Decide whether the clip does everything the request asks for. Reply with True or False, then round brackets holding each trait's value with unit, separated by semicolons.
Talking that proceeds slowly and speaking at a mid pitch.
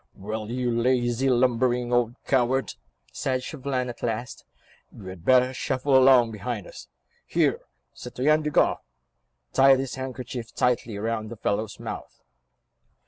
False (130 wpm; 125 Hz)